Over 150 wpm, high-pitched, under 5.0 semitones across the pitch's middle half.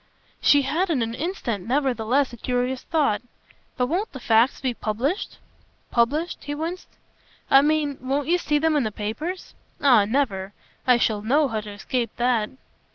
Yes: average, 165 wpm; very high, 260 Hz; average, 4.6 semitones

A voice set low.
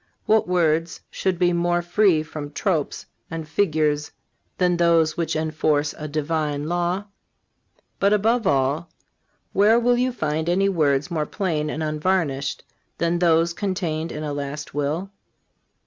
No: medium, 165 Hz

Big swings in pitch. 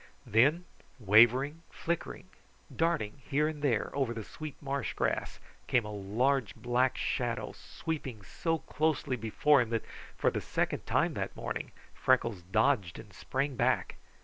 No: average, 4.6 semitones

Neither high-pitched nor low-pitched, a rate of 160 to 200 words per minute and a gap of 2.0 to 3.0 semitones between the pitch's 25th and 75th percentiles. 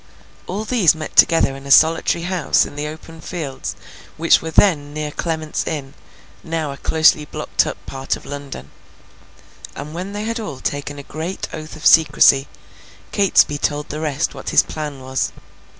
Yes: medium, 155 Hz; average, 170 wpm; narrow, 2.5 semitones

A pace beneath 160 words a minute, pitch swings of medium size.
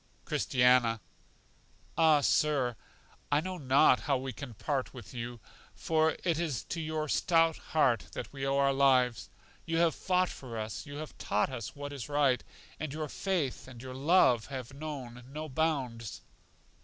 No: average, 165 wpm; average, 3.8 semitones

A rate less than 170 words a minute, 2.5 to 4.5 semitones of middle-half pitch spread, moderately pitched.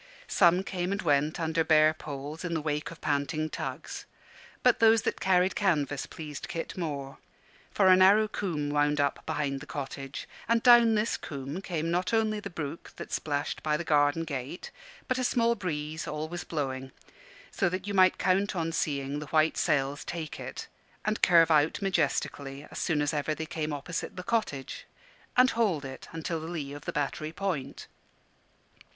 No: average, 180 wpm; average, 4.2 semitones; medium, 160 Hz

